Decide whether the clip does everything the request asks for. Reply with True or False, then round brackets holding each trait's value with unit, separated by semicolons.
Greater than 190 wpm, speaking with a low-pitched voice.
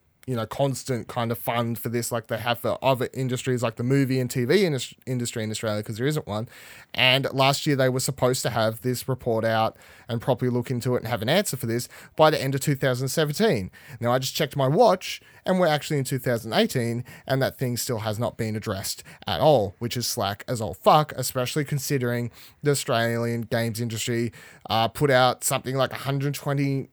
True (205 wpm; 125 Hz)